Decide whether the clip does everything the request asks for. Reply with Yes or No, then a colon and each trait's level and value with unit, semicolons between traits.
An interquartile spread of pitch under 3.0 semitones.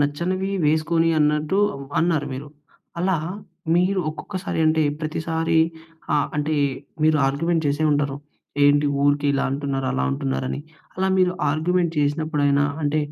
Yes: narrow, 2.6 semitones